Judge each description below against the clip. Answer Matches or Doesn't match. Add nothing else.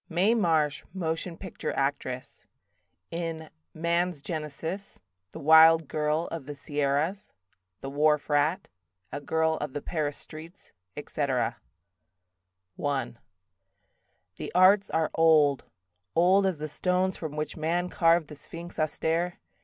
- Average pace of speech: Doesn't match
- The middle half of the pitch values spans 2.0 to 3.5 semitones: Matches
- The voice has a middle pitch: Matches